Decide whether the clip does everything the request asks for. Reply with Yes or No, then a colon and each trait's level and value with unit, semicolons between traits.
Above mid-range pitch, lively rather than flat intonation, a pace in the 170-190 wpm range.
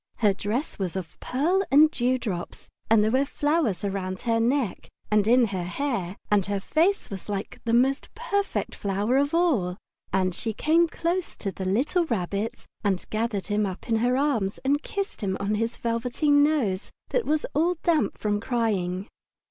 Yes: high, 230 Hz; wide, 6.5 semitones; average, 180 wpm